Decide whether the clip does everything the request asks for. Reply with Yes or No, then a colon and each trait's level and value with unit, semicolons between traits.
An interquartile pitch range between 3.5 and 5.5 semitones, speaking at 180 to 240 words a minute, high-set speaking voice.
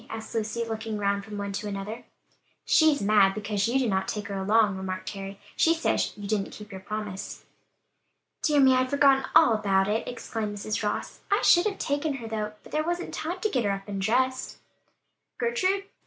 Yes: average, 5.0 semitones; average, 200 wpm; high, 215 Hz